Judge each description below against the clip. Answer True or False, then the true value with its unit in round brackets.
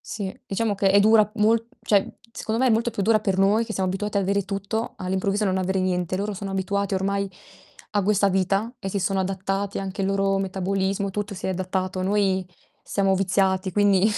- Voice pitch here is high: True (195 Hz)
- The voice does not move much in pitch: True (1.4 semitones)